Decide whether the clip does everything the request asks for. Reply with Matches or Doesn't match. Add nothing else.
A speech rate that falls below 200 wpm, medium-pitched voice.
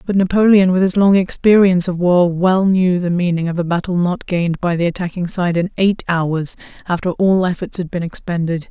Doesn't match